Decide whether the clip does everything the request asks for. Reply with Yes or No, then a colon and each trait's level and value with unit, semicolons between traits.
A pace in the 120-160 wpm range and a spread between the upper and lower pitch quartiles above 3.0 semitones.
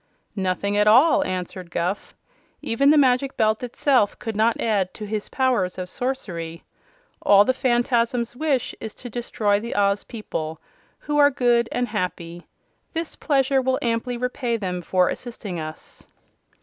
Yes: average, 150 wpm; average, 4.3 semitones